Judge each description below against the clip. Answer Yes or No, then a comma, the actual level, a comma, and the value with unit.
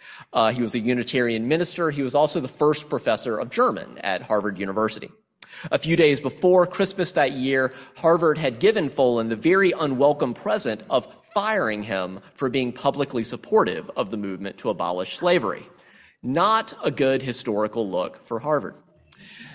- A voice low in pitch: Yes, low, 130 Hz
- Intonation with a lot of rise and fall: Yes, wide, 5.9 semitones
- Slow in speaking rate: No, average, 160 wpm